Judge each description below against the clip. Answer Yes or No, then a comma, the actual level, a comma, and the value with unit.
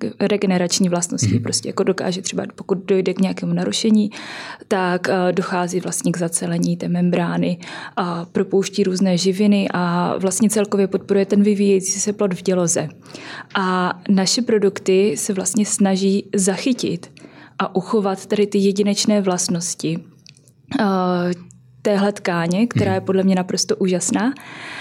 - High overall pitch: Yes, high, 195 Hz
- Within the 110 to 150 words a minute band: Yes, average, 130 wpm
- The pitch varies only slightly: Yes, narrow, 2.3 semitones